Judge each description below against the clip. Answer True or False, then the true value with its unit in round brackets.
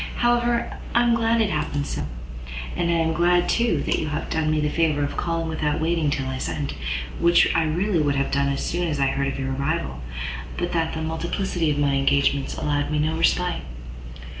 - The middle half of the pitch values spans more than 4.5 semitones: False (3.2 semitones)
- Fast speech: True (215 wpm)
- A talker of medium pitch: True (160 Hz)